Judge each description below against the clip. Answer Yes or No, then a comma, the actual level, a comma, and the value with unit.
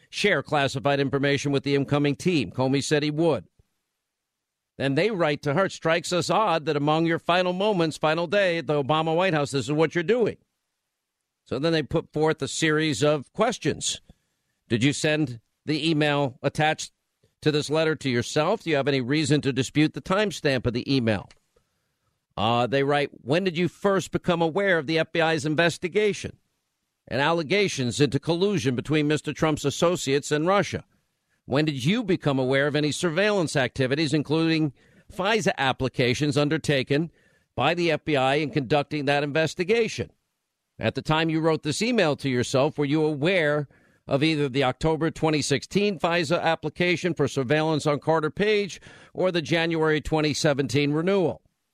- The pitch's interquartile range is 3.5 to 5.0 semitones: No, average, 2.8 semitones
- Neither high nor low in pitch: Yes, medium, 155 Hz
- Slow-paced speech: No, average, 165 wpm